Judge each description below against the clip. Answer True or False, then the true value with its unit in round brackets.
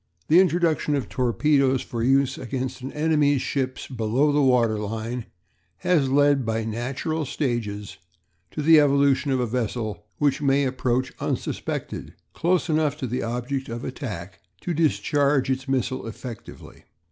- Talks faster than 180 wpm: False (140 wpm)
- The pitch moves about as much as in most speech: True (3.4 semitones)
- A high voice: False (130 Hz)